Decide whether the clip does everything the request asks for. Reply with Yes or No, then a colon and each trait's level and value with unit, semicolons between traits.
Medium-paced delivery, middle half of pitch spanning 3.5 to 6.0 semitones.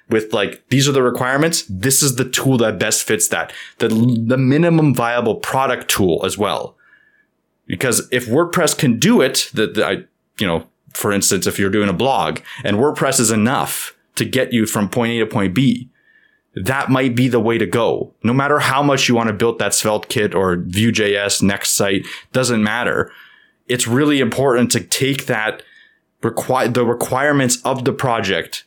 No: average, 185 wpm; average, 2.8 semitones